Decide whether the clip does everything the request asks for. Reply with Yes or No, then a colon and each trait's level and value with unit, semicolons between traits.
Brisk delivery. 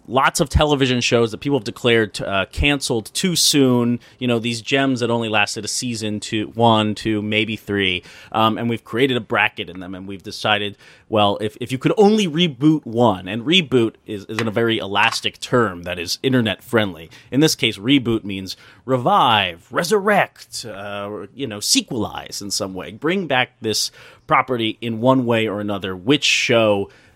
No: average, 185 wpm